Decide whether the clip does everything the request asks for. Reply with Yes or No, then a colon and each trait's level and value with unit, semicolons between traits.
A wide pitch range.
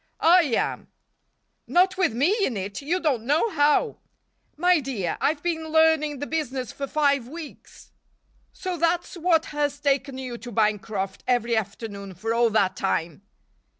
Yes: wide, 6.3 semitones